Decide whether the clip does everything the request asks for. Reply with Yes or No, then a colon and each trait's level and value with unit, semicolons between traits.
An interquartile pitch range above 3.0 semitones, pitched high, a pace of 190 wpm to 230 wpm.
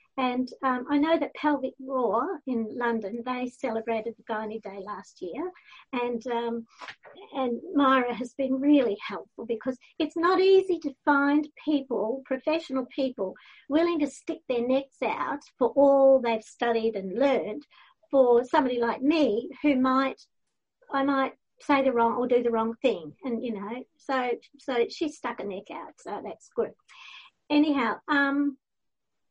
No: average, 3.7 semitones; very high, 265 Hz; average, 155 wpm